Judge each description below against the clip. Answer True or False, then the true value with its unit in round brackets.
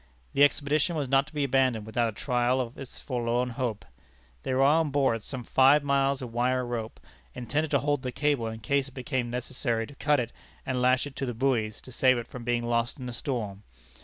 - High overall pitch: False (130 Hz)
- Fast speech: True (220 wpm)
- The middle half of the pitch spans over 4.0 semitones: False (2.6 semitones)